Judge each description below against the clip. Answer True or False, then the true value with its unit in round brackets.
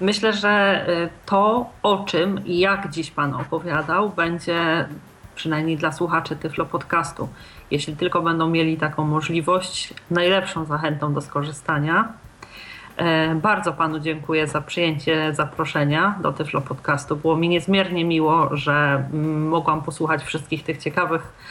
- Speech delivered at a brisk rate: False (125 wpm)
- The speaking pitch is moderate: True (160 Hz)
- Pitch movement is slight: True (2.0 semitones)